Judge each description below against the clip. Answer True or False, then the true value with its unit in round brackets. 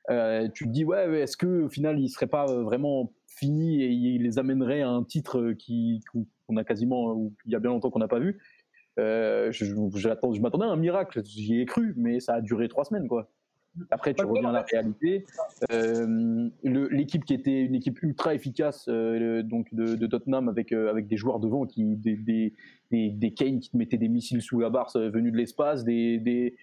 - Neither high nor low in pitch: False (120 Hz)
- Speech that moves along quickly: True (230 wpm)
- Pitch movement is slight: False (3.3 semitones)